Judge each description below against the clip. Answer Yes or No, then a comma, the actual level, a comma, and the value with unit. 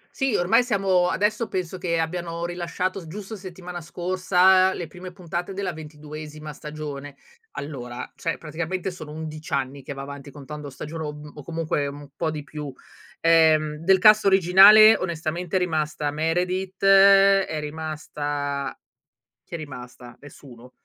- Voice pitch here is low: No, medium, 165 Hz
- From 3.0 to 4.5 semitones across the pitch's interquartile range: Yes, average, 3.7 semitones